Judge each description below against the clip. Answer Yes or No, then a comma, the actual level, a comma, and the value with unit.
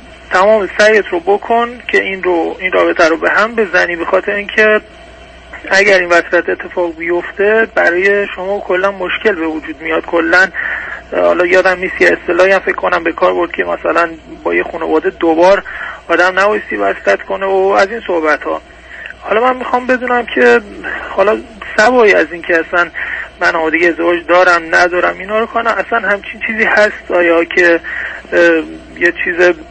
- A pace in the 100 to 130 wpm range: No, fast, 165 wpm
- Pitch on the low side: No, medium, 185 Hz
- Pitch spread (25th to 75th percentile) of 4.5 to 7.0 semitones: No, average, 3.7 semitones